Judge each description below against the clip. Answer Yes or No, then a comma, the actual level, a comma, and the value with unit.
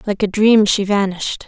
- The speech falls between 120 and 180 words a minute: No, fast, 205 wpm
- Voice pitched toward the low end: No, high, 205 Hz